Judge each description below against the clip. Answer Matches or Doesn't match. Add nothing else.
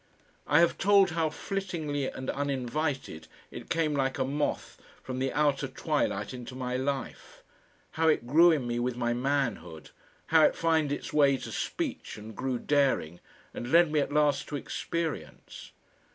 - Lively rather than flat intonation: Doesn't match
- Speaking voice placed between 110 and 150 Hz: Matches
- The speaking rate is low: Doesn't match